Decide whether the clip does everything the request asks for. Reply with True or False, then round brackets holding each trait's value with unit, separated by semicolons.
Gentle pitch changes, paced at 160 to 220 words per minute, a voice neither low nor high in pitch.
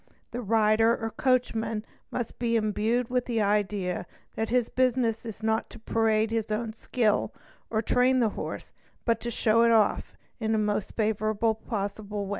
False (1.6 semitones; 175 wpm; 225 Hz)